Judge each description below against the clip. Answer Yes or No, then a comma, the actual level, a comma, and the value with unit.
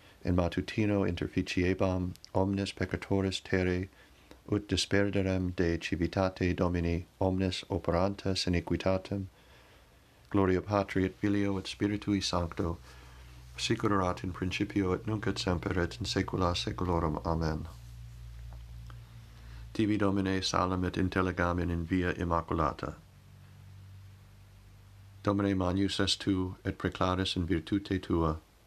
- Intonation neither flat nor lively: No, narrow, 2.3 semitones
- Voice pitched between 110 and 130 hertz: No, very low, 95 Hz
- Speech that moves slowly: Yes, slow, 105 wpm